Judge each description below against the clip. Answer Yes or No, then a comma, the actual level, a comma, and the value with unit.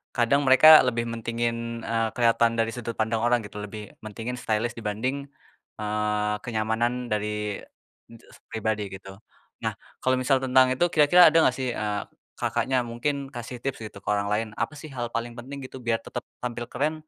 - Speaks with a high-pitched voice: No, low, 115 Hz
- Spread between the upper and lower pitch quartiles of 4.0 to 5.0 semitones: No, average, 2.8 semitones